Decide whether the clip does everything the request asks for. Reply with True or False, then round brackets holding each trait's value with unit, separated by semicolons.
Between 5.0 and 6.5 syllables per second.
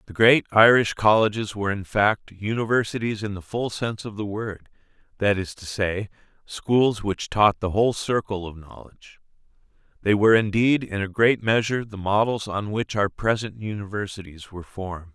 True (5.1 syllables/s)